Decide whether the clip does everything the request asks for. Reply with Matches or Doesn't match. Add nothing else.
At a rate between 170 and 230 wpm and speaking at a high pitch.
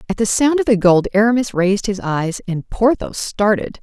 Matches